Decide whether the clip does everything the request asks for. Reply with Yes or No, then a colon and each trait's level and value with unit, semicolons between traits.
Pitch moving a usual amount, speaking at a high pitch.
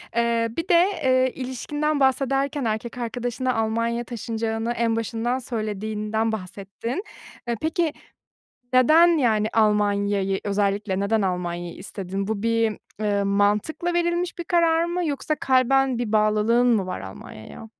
Yes: average, 4.1 semitones; high, 230 Hz